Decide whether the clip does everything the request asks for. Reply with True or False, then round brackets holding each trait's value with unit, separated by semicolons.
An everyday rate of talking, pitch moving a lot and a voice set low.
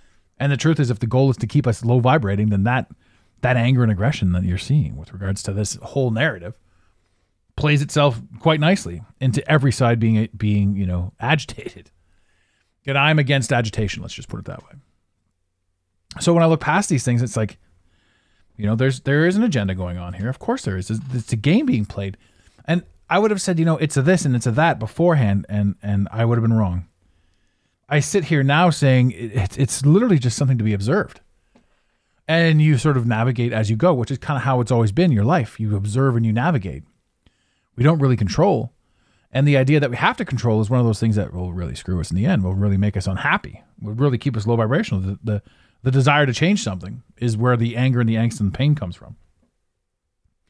False (225 wpm; 5.8 semitones; 115 Hz)